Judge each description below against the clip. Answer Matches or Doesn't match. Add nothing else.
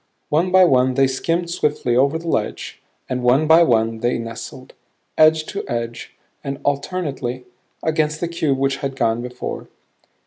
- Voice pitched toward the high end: Doesn't match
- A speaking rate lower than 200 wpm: Matches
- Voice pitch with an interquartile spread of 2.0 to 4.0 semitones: Doesn't match